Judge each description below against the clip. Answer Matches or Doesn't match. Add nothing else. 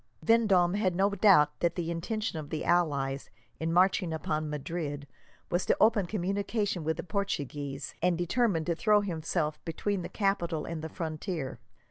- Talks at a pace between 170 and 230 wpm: Doesn't match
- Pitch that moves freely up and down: Doesn't match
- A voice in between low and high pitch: Matches